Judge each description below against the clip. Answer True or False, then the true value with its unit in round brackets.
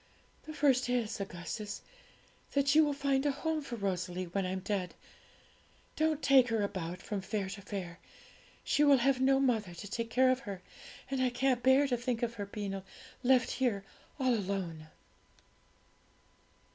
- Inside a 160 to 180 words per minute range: True (165 wpm)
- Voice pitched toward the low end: False (235 Hz)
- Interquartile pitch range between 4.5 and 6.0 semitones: True (5.4 semitones)